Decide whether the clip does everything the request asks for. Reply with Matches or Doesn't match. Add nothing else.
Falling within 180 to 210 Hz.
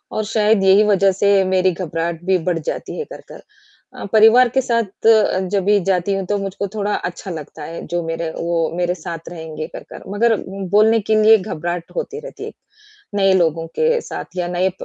Matches